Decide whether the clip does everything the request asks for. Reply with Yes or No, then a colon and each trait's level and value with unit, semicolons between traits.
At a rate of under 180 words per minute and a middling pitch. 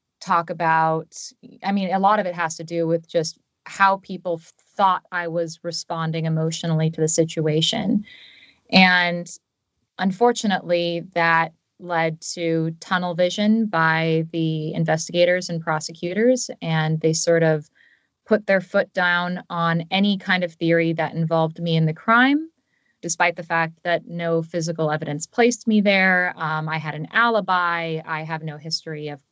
Yes: average, 150 wpm; medium, 170 Hz